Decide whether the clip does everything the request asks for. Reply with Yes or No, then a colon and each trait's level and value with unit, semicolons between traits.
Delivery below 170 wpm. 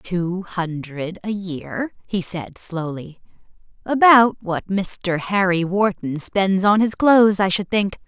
Yes: average, 140 wpm